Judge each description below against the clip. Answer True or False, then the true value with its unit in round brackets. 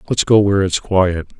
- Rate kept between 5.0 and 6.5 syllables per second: True (5.4 syllables/s)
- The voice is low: True (95 Hz)